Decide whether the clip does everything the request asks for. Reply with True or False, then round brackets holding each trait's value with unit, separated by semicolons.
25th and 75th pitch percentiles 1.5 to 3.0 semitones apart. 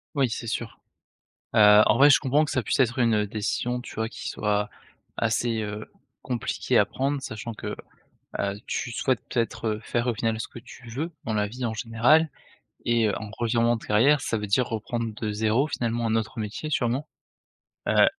True (2.5 semitones)